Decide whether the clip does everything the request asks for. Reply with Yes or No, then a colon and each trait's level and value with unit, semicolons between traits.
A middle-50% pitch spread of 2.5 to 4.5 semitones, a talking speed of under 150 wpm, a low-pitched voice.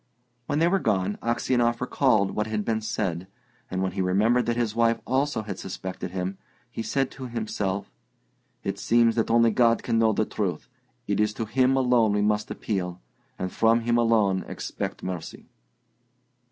No: average, 3.2 semitones; average, 175 wpm; low, 110 Hz